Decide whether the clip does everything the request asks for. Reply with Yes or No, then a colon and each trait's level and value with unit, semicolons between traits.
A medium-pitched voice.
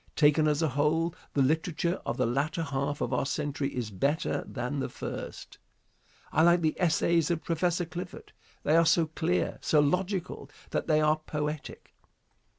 Yes: medium, 155 Hz